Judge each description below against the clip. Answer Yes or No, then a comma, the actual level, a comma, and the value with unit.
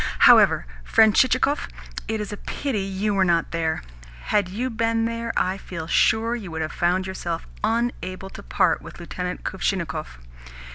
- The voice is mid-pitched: No, high, 195 Hz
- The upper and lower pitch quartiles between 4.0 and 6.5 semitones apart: Yes, average, 4.5 semitones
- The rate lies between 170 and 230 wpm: No, average, 160 wpm